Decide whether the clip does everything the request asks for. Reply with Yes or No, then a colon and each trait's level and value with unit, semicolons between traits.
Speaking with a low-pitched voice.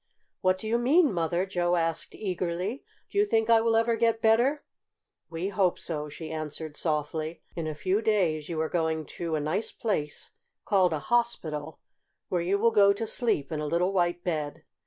No: medium, 175 Hz